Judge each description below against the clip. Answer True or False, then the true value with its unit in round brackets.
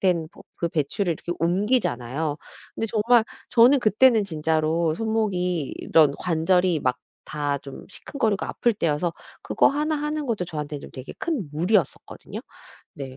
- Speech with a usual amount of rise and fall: False (6.4 semitones)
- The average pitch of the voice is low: False (180 Hz)